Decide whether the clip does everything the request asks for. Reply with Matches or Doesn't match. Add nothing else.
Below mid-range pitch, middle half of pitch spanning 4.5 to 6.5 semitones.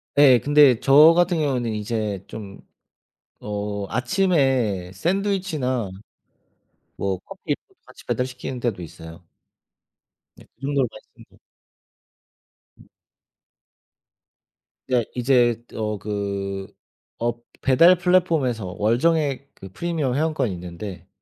Matches